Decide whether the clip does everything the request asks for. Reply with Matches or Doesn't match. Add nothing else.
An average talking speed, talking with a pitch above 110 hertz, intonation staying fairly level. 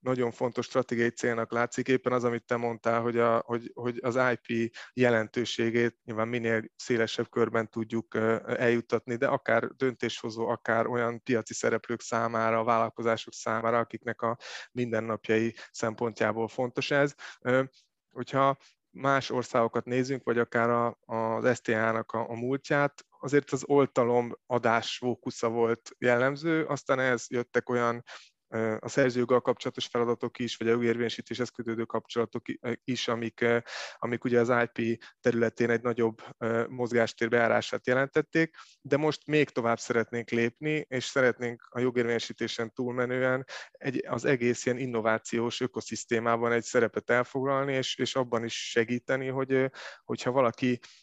Matches